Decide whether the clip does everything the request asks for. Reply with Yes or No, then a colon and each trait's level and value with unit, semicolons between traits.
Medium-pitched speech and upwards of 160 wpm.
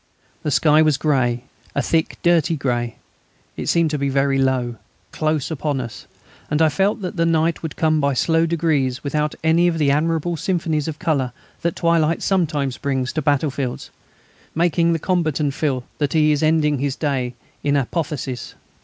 Yes: medium, 150 Hz; average, 170 wpm